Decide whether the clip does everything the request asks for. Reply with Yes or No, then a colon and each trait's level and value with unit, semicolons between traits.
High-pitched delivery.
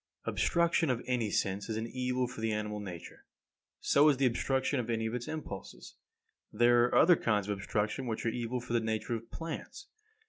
No: low, 120 Hz